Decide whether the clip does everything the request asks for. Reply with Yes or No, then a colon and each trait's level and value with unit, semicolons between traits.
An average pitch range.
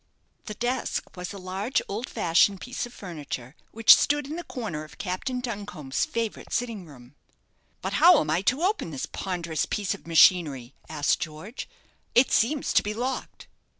No: wide, 7.2 semitones